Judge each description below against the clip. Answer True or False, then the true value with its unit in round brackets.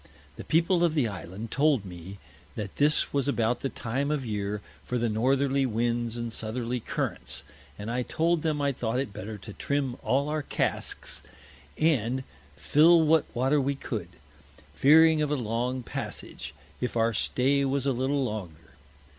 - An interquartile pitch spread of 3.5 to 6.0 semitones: True (4.2 semitones)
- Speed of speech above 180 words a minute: False (165 wpm)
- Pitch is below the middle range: True (125 Hz)